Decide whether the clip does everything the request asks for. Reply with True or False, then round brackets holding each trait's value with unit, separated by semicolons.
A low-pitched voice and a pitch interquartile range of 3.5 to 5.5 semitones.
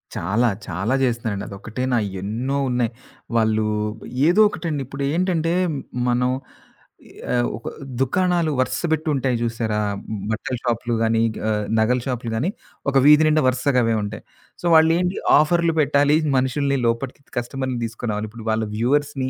True (125 Hz; 4.4 semitones)